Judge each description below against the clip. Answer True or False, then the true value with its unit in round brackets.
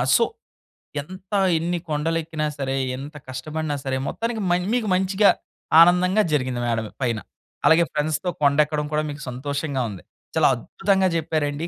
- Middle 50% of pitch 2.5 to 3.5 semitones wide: False (4.0 semitones)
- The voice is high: False (155 Hz)